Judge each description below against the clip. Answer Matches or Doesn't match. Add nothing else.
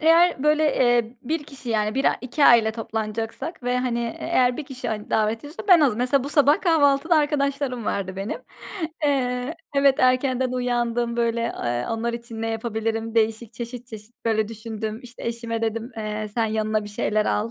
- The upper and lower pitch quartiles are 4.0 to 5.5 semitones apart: Doesn't match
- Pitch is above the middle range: Matches